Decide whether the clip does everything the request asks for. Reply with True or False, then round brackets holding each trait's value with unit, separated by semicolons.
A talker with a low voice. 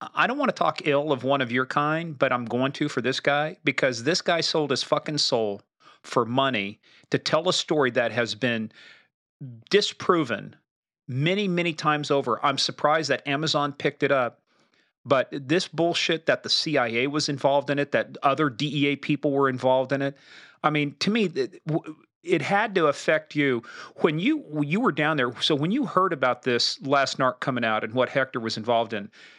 False (145 Hz)